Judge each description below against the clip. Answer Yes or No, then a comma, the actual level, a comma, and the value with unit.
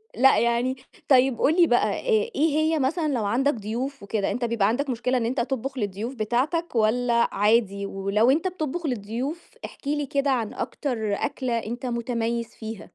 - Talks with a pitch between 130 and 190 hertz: No, high, 245 Hz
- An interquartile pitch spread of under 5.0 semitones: Yes, average, 3.9 semitones